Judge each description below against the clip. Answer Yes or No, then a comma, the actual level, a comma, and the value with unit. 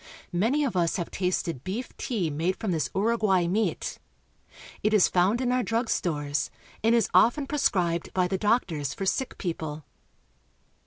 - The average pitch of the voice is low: No, high, 190 Hz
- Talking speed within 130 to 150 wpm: No, average, 160 wpm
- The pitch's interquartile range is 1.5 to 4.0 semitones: No, average, 5.2 semitones